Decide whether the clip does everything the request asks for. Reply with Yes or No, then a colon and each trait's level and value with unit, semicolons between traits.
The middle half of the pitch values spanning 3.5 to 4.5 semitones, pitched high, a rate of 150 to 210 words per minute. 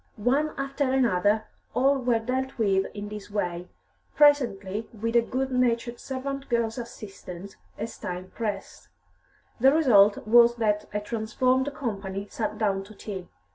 No: average, 4.1 semitones; high, 230 Hz; average, 140 wpm